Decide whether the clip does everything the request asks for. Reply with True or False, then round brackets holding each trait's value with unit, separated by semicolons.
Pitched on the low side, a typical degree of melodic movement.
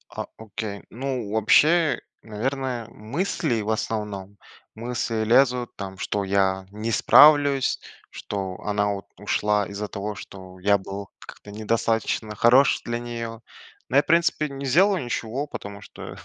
True (110 Hz; 4.1 semitones)